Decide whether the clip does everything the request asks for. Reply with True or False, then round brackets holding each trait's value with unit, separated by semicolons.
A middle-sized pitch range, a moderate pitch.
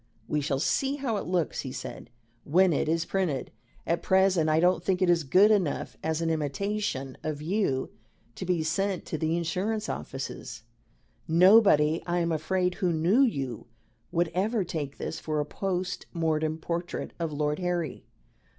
True (3.5 semitones; 170 Hz)